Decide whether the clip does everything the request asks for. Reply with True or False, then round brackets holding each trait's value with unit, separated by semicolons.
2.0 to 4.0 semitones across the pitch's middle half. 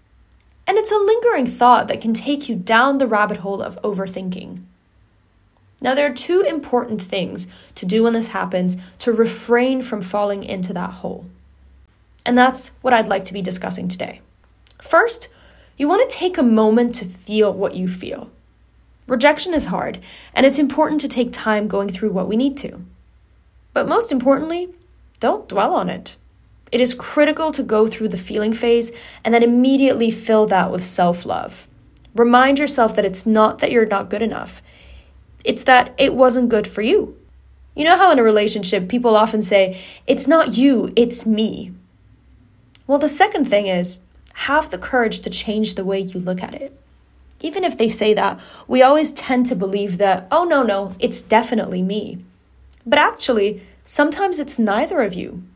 False (5.5 semitones)